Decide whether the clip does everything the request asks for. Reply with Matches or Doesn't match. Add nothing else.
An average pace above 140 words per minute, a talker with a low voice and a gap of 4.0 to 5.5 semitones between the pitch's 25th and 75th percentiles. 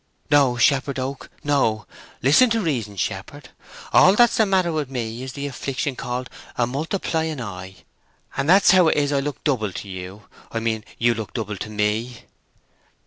Matches